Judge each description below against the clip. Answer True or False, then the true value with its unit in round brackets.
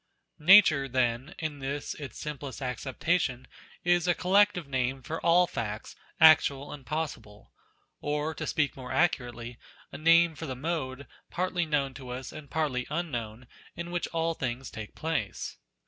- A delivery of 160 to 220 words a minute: False (150 wpm)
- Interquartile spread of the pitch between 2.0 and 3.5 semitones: False (4.3 semitones)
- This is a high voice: False (145 Hz)